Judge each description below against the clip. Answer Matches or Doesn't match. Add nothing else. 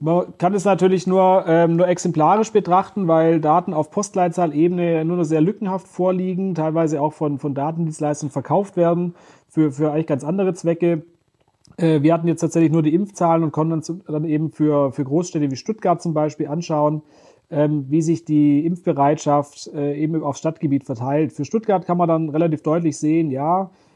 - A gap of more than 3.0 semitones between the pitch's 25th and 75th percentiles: Doesn't match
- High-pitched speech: Doesn't match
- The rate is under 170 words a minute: Doesn't match